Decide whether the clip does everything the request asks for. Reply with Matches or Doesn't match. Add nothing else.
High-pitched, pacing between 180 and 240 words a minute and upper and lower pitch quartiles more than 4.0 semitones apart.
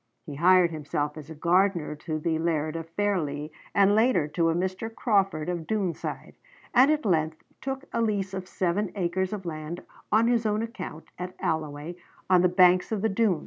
Doesn't match